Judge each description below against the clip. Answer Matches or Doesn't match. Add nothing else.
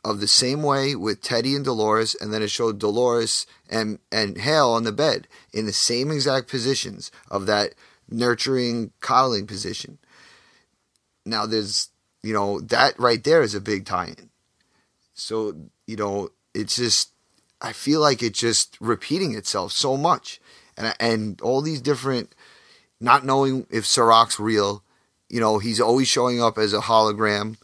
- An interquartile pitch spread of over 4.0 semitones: Doesn't match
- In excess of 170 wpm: Doesn't match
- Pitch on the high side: Doesn't match